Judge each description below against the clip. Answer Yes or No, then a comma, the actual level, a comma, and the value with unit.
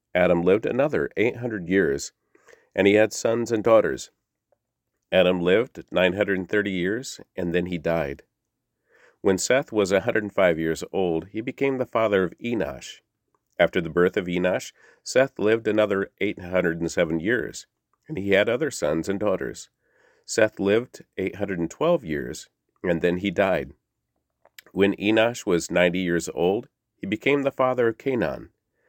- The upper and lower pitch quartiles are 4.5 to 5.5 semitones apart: No, average, 3.6 semitones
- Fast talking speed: No, average, 170 wpm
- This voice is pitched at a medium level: No, very low, 95 Hz